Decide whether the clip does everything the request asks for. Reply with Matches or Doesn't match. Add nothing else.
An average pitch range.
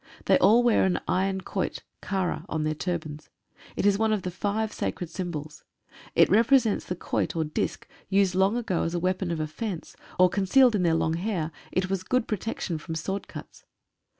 Matches